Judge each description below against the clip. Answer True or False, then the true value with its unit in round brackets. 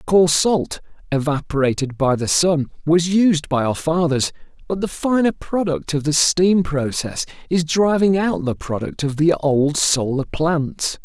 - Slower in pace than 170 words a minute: True (160 wpm)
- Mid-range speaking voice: True (160 Hz)